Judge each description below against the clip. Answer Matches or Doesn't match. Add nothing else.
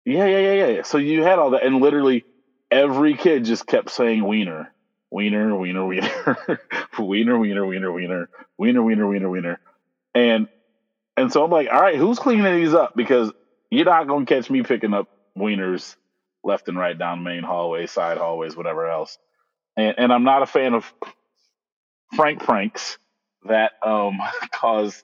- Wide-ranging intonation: Matches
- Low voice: Matches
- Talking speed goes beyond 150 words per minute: Matches